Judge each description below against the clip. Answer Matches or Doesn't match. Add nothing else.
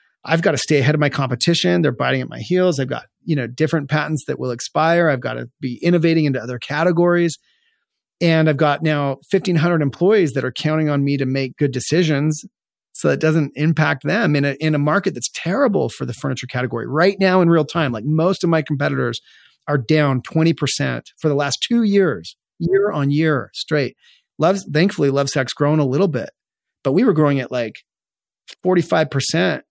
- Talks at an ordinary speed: Doesn't match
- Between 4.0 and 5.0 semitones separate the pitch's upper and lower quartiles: Doesn't match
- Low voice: Doesn't match